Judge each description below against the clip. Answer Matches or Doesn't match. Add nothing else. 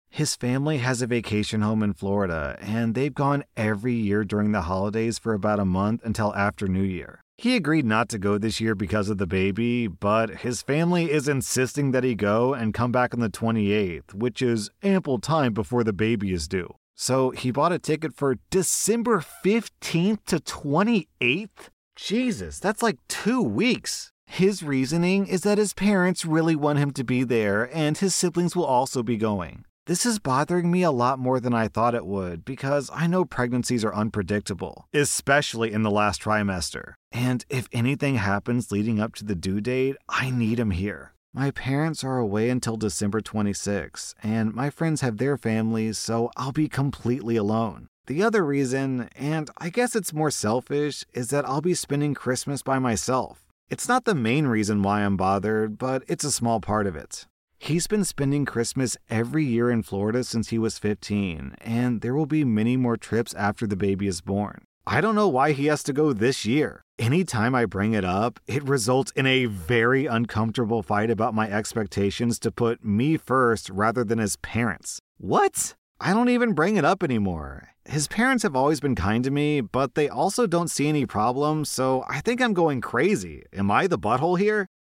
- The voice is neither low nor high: Doesn't match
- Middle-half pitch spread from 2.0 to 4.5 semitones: Doesn't match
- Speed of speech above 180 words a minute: Matches